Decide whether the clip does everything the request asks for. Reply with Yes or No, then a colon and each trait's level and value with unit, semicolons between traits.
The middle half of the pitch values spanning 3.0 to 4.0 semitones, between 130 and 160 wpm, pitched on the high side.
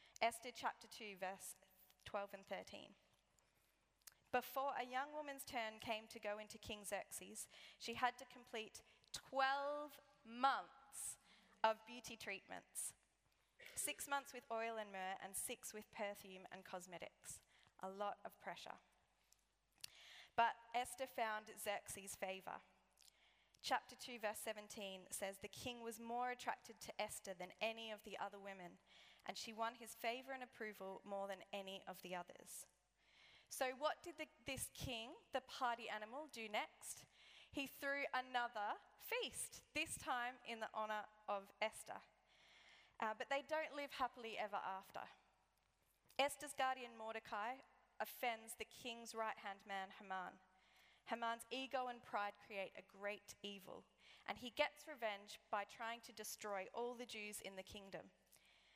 Yes: average, 3.7 semitones; average, 145 wpm; high, 225 Hz